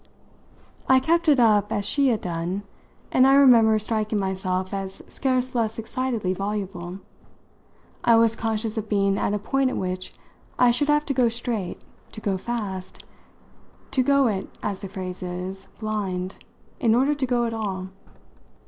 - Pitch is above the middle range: Yes, high, 215 Hz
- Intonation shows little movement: No, average, 4.4 semitones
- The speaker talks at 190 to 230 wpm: No, average, 165 wpm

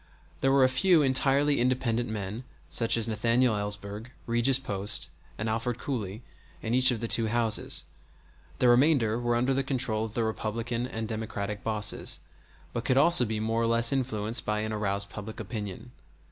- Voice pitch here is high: No, low, 115 Hz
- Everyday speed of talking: Yes, average, 175 wpm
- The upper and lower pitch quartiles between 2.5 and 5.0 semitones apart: Yes, average, 2.8 semitones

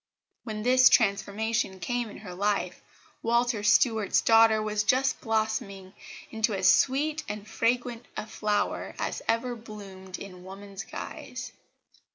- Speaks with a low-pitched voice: No, high, 215 Hz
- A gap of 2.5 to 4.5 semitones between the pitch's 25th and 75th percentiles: Yes, average, 2.8 semitones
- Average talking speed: No, slow, 130 wpm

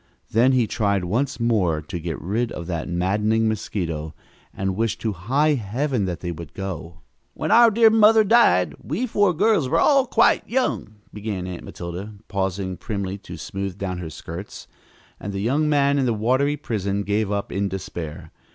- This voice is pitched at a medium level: No, low, 105 Hz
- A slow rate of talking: No, average, 180 wpm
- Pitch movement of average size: No, wide, 6.7 semitones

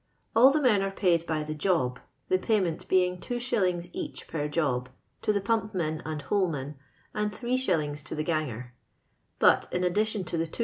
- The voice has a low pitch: No, medium, 175 Hz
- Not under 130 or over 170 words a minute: No, average, 180 wpm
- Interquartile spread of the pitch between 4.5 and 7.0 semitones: Yes, wide, 5.4 semitones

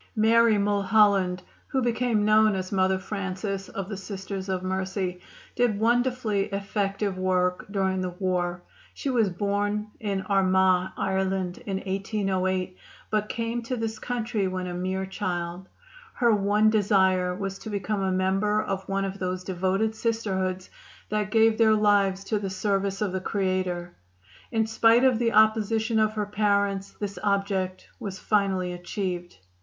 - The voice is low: No, high, 195 Hz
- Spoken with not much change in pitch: Yes, narrow, 2.3 semitones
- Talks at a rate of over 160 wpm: No, average, 150 wpm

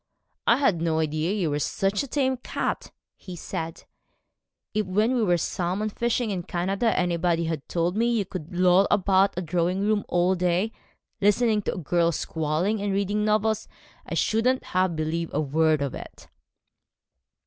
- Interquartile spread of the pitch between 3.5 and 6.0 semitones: Yes, average, 4.0 semitones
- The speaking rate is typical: Yes, average, 170 wpm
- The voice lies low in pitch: No, medium, 185 Hz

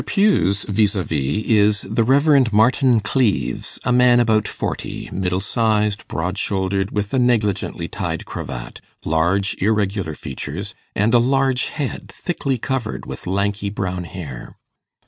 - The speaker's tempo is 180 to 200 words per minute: No, average, 140 wpm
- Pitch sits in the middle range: No, low, 105 Hz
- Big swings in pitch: No, average, 4.2 semitones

